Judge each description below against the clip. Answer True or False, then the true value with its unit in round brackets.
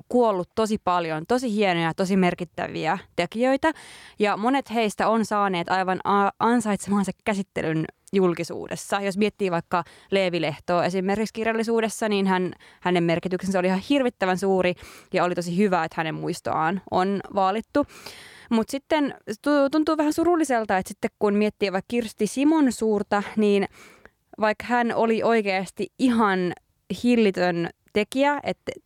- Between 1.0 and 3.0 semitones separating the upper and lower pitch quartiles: False (3.7 semitones)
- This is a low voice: False (200 Hz)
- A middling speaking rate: True (130 wpm)